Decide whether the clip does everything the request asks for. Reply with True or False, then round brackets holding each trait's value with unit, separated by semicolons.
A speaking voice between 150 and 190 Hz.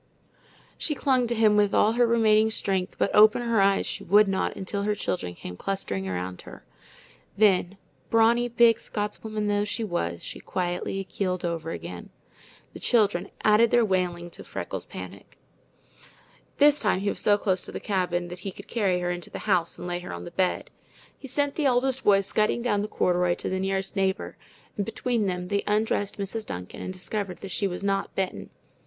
False (200 Hz)